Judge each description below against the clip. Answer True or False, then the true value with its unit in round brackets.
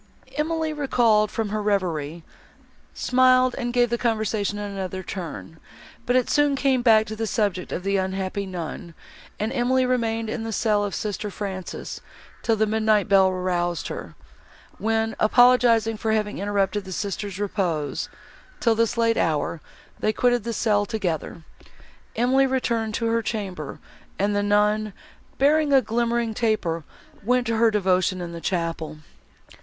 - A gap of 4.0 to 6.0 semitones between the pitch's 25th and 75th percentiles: False (3.6 semitones)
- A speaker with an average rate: True (150 wpm)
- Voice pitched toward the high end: True (215 Hz)